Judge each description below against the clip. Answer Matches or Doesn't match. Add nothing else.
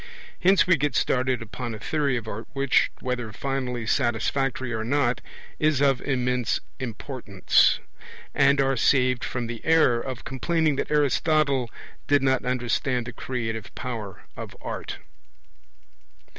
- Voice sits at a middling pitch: Doesn't match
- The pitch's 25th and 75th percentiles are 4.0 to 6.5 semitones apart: Doesn't match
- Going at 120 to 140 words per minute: Matches